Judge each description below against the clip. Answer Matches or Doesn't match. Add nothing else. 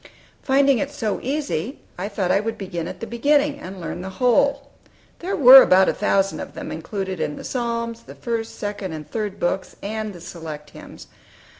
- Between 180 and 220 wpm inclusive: Matches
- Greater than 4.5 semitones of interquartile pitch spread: Matches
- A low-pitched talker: Doesn't match